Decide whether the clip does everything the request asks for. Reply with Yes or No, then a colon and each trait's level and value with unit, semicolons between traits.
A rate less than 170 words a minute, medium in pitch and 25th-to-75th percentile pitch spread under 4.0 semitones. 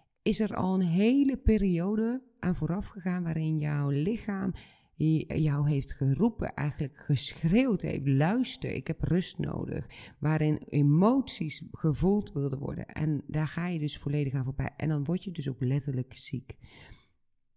No: average, 150 wpm; medium, 155 Hz; average, 4.9 semitones